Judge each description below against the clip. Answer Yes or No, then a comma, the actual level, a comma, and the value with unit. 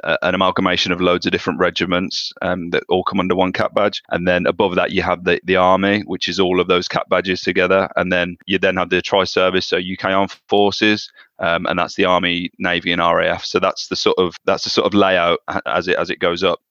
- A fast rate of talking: Yes, fast, 240 wpm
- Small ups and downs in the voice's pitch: Yes, narrow, 1.3 semitones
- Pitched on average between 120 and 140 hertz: No, very low, 90 Hz